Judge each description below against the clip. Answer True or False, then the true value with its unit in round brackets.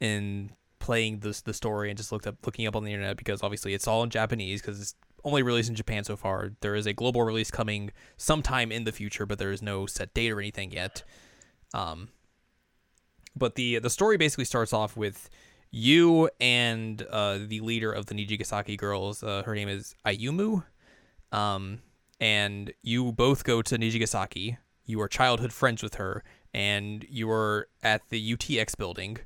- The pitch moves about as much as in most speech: False (2.3 semitones)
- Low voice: True (110 Hz)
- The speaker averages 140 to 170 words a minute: False (185 wpm)